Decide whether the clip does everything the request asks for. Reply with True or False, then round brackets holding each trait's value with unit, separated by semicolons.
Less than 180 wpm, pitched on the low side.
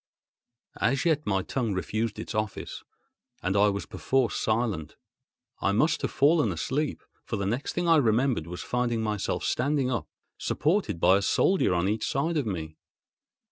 True (165 wpm; 115 Hz)